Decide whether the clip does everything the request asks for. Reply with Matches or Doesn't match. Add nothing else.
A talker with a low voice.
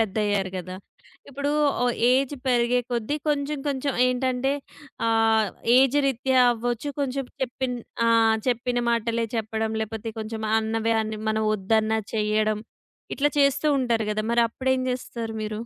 Doesn't match